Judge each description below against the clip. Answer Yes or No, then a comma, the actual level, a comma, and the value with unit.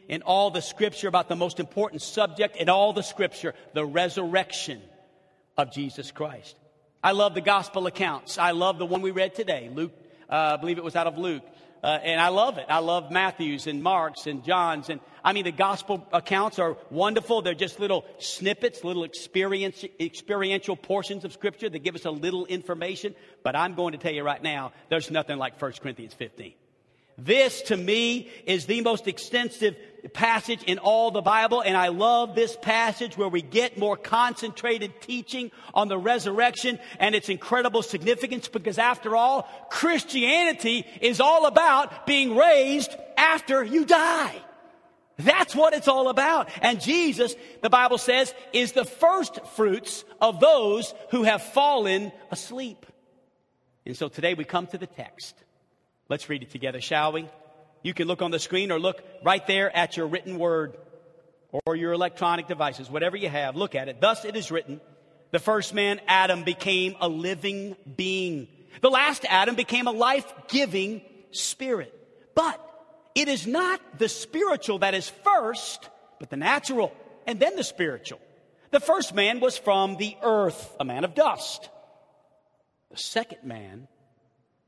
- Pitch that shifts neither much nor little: No, wide, 5.9 semitones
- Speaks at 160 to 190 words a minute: Yes, average, 170 wpm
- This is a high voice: Yes, high, 195 Hz